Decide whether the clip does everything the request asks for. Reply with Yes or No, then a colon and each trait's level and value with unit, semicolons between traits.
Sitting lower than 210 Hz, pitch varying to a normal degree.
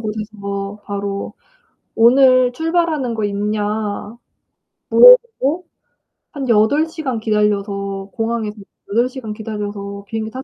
No: high, 220 Hz; average, 3.9 semitones